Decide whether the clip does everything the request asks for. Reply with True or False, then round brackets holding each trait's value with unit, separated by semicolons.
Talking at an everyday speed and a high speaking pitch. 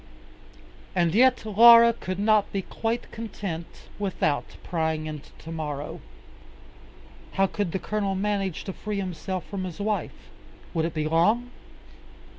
False (130 wpm; 195 Hz)